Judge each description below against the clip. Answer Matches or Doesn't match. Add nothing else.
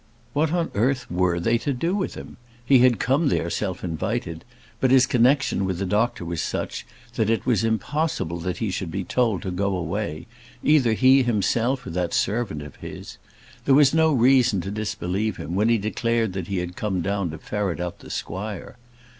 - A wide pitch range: Matches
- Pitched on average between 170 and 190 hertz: Doesn't match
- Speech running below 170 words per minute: Doesn't match